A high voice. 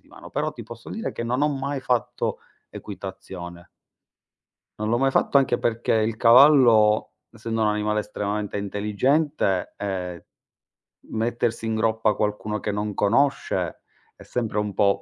No: low, 110 Hz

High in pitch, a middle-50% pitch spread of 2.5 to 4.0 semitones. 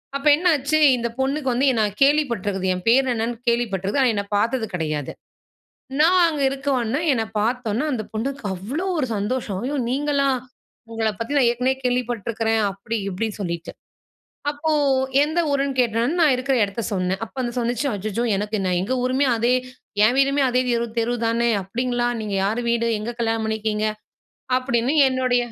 Yes: high, 240 Hz; average, 3.7 semitones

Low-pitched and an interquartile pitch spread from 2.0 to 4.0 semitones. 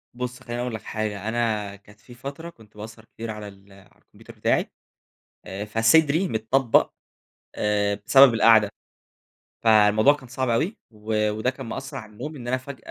Yes: low, 115 Hz; average, 3.4 semitones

